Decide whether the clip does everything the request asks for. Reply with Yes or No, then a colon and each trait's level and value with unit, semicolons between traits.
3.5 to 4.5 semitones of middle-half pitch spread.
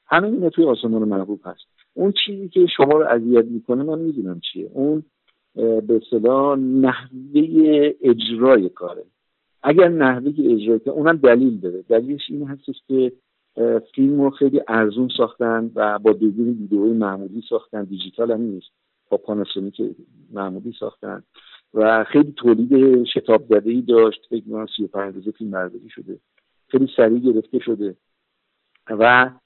Yes: average, 4.2 semitones